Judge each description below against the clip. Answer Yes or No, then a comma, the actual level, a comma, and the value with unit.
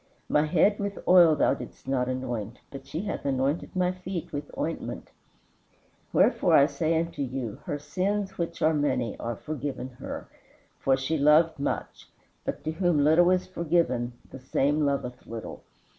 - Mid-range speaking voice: Yes, medium, 150 Hz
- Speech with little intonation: No, average, 4.3 semitones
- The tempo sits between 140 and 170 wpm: Yes, average, 160 wpm